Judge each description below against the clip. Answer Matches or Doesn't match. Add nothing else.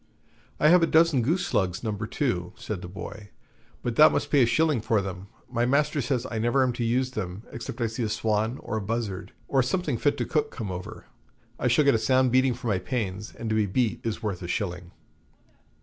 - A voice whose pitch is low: Matches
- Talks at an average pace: Doesn't match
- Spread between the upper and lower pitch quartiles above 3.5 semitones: Matches